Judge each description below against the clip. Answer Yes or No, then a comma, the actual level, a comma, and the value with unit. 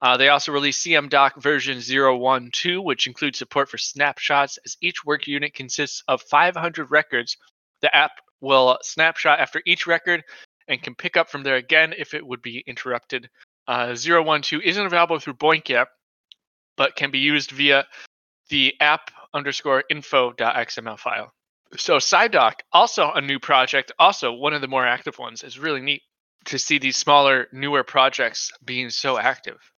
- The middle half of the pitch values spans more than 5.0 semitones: No, average, 2.8 semitones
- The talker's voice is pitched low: No, medium, 145 Hz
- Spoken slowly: No, average, 165 wpm